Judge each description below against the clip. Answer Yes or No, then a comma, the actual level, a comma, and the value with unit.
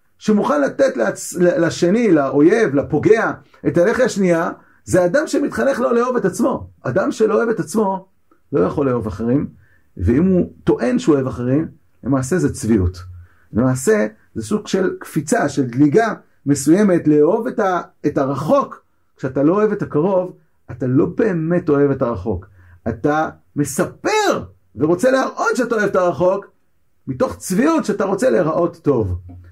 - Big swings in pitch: Yes, wide, 8.1 semitones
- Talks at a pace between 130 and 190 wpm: Yes, average, 145 wpm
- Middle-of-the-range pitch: Yes, medium, 170 Hz